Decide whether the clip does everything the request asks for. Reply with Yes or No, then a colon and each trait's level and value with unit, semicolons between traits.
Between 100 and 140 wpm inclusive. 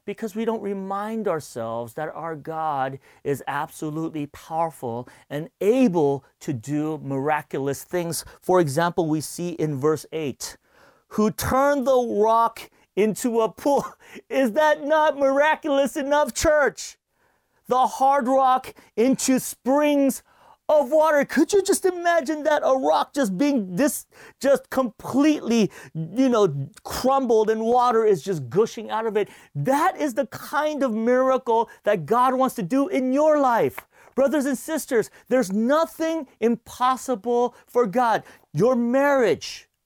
Yes: slow, 135 wpm